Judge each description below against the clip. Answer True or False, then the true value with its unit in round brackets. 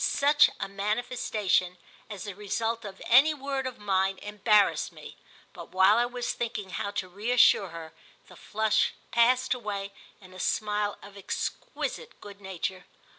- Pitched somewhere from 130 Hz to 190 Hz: False (210 Hz)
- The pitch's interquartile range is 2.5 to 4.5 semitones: True (3.6 semitones)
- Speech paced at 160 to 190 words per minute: False (150 wpm)